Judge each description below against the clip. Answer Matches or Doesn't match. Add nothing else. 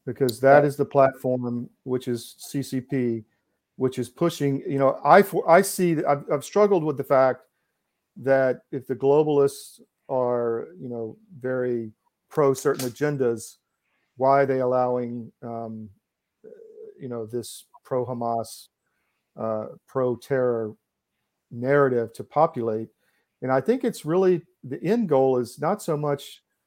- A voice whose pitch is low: Matches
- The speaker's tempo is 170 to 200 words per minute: Doesn't match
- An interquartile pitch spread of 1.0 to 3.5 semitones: Matches